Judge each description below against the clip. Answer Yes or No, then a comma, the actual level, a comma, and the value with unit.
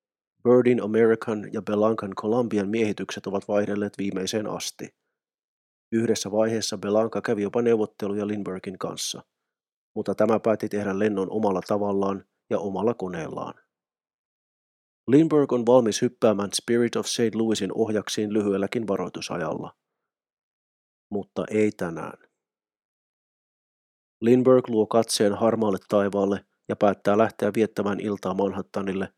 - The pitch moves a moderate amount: No, narrow, 2.1 semitones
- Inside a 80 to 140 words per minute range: Yes, average, 110 wpm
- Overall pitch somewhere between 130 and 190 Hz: No, low, 105 Hz